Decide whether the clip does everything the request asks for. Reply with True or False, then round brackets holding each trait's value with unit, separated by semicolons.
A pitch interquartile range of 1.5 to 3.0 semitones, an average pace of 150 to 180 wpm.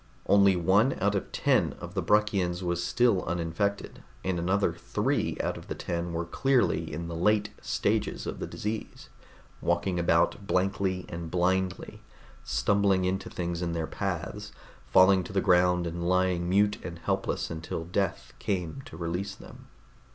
True (2.5 semitones; 160 wpm)